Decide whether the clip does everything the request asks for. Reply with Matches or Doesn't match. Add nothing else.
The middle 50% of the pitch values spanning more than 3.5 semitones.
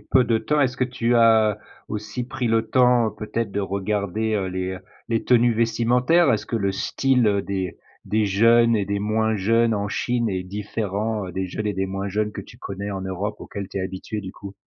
Doesn't match